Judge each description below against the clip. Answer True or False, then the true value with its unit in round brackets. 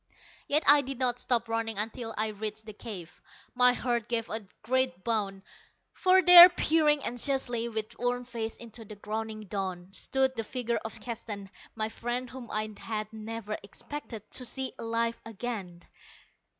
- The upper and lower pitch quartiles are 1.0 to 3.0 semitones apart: True (2.5 semitones)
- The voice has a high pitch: True (230 Hz)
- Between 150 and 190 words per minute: True (160 wpm)